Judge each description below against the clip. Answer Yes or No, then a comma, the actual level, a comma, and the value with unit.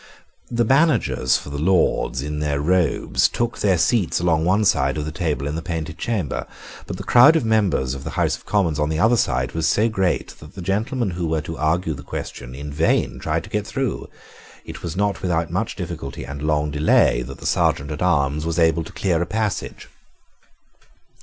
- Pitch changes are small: No, average, 5.0 semitones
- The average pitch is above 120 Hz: No, very low, 80 Hz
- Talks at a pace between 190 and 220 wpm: Yes, fast, 205 wpm